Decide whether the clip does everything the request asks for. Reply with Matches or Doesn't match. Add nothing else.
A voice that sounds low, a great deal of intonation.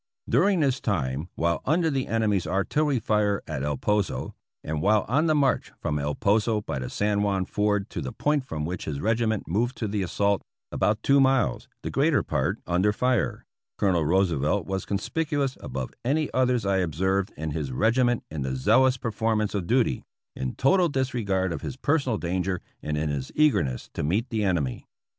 Matches